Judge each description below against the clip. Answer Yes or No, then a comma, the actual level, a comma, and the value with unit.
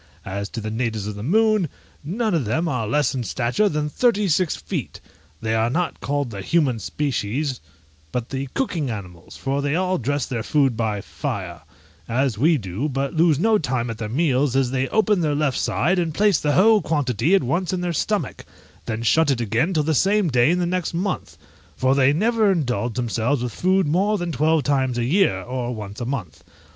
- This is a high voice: No, medium, 140 Hz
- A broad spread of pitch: Yes, wide, 6.3 semitones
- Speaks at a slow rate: No, fast, 205 wpm